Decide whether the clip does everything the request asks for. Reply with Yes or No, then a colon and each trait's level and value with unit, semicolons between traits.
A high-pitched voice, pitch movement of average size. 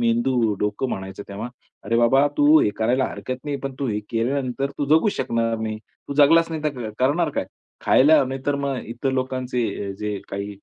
No: low, 125 Hz; average, 3.8 semitones